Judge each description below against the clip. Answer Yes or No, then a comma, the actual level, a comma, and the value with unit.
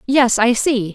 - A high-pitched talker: Yes, high, 240 Hz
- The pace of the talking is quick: No, average, 190 wpm